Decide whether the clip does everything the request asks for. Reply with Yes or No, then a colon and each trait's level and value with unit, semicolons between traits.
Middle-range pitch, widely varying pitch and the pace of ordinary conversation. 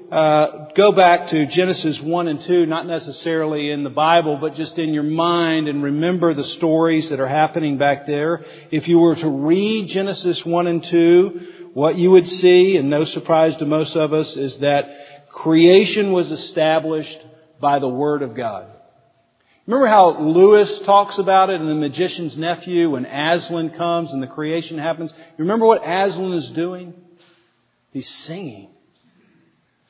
No: medium, 160 Hz; narrow, 2.5 semitones; average, 165 wpm